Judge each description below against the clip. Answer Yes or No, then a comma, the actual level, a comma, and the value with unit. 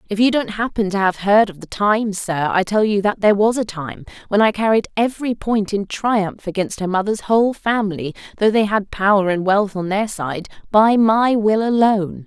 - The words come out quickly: Yes, fast, 215 wpm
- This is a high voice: Yes, high, 205 Hz